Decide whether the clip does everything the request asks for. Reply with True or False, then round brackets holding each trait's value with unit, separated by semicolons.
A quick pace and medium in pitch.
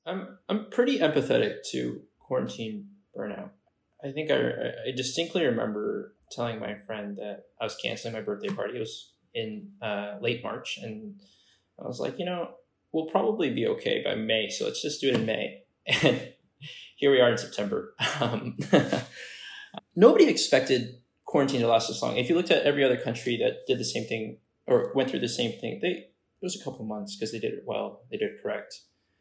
False (195 wpm; 145 Hz)